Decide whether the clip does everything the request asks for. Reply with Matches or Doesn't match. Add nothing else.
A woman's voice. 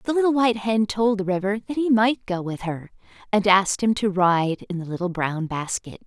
Matches